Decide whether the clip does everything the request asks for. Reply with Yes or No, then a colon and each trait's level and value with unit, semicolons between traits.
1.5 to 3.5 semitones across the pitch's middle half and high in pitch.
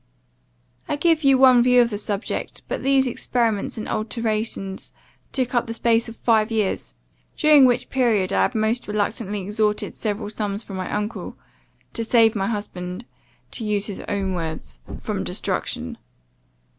Yes: average, 2.8 semitones; high, 220 Hz